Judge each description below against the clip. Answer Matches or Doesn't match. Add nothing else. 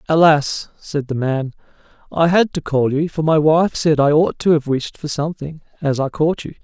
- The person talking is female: Doesn't match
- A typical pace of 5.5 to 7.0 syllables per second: Doesn't match